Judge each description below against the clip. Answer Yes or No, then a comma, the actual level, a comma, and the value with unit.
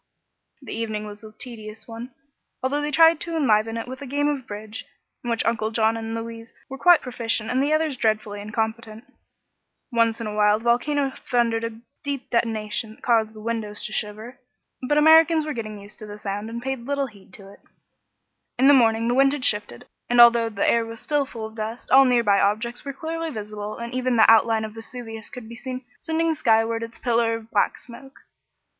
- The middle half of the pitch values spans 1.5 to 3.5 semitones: Yes, average, 3.1 semitones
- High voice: Yes, high, 230 Hz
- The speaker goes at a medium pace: No, fast, 210 wpm